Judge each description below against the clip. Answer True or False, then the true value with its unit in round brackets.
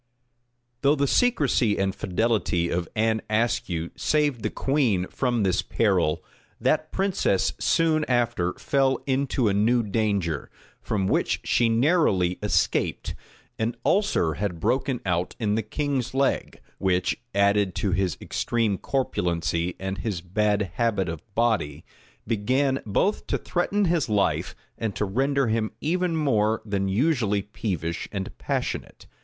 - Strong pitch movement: True (5.7 semitones)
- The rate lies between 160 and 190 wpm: False (135 wpm)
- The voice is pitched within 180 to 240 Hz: False (110 Hz)